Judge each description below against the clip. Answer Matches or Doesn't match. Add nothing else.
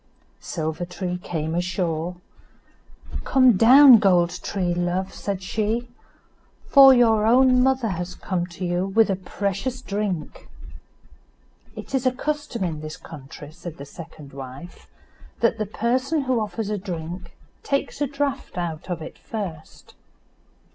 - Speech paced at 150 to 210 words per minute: Doesn't match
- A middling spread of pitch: Doesn't match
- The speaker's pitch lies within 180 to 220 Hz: Matches